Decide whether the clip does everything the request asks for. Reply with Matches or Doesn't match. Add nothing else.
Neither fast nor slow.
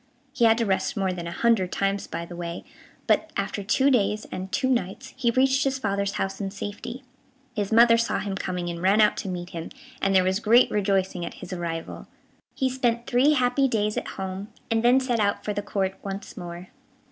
Doesn't match